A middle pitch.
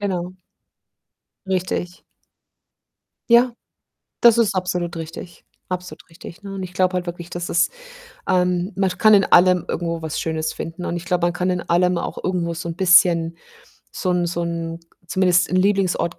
Yes: medium, 180 Hz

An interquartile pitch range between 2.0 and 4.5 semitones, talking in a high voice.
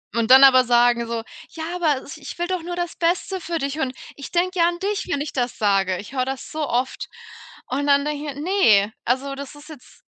No: average, 5.0 semitones; very high, 280 Hz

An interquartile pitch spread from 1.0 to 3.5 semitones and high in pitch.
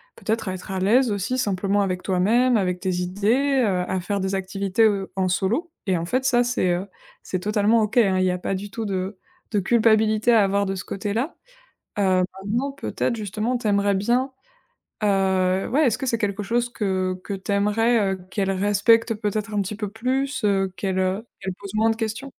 Yes: average, 3.1 semitones; high, 205 Hz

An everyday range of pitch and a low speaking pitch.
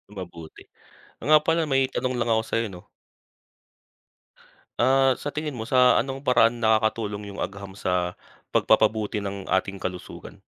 Yes: average, 4.7 semitones; low, 110 Hz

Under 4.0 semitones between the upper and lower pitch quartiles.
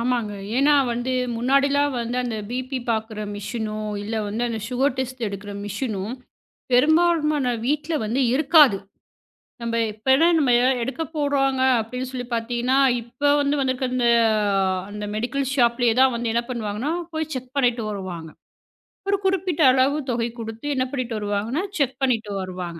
Yes: average, 3.6 semitones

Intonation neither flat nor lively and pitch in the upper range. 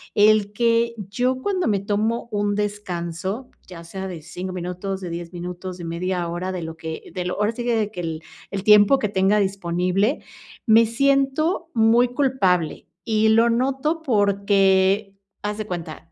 Yes: average, 4.2 semitones; high, 200 Hz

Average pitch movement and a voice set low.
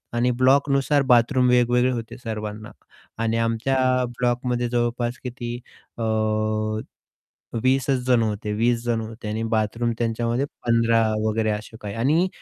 No: narrow, 1.8 semitones; low, 120 Hz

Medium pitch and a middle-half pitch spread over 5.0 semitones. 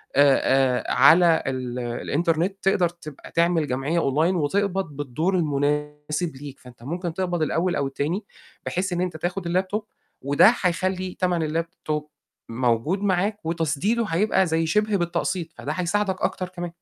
No: medium, 170 Hz; average, 4.0 semitones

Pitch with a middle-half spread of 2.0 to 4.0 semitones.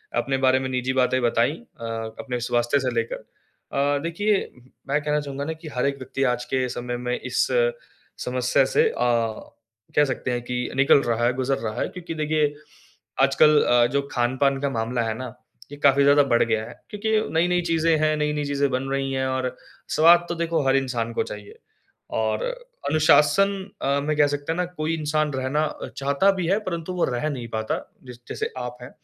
Yes: average, 3.7 semitones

